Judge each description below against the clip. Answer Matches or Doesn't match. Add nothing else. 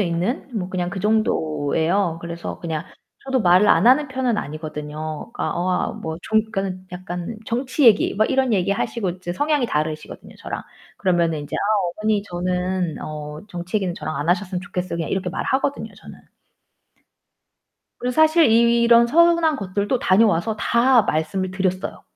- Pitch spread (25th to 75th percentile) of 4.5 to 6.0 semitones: Matches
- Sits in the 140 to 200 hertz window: Matches